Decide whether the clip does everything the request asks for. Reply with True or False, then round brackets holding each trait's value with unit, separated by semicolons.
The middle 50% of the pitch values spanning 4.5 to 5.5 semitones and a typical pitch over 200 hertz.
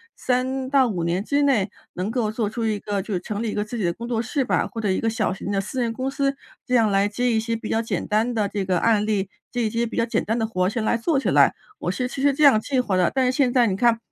False (3.4 semitones; 225 Hz)